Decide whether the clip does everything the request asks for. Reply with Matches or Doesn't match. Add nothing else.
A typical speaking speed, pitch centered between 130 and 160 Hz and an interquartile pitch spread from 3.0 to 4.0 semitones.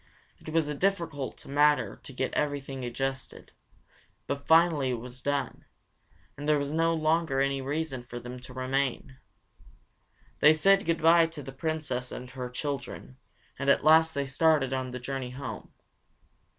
Matches